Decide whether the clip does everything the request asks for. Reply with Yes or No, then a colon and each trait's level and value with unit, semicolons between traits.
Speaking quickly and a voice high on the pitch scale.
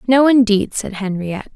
No: average, 155 wpm; high, 220 Hz